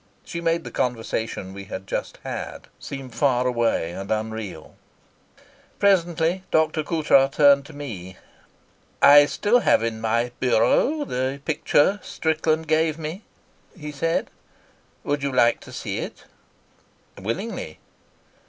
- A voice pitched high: No, medium, 140 Hz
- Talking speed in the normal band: No, slow, 125 wpm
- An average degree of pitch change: No, wide, 5.8 semitones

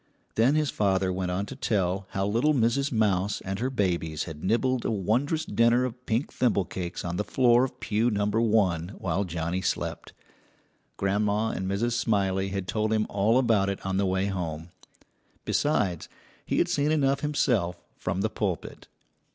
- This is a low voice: Yes, low, 105 Hz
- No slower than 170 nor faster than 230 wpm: Yes, average, 175 wpm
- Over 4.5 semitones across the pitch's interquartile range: No, average, 3.9 semitones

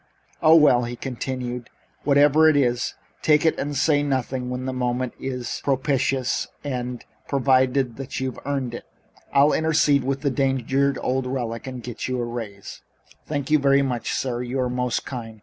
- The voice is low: Yes, low, 130 Hz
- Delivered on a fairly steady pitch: Yes, narrow, 2.1 semitones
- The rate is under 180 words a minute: Yes, average, 170 wpm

